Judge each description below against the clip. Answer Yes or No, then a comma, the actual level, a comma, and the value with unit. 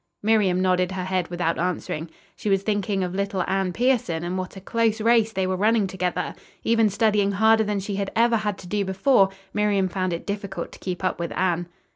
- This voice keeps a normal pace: No, fast, 210 wpm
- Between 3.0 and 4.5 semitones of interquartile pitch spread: No, narrow, 2.4 semitones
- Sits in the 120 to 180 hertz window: No, high, 195 Hz